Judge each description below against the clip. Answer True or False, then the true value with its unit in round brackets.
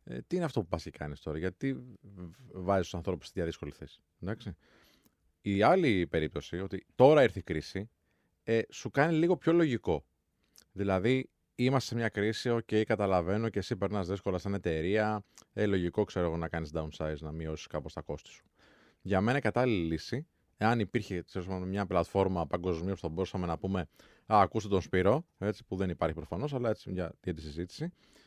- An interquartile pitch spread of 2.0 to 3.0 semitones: False (4.5 semitones)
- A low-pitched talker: True (95 Hz)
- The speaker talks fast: True (185 wpm)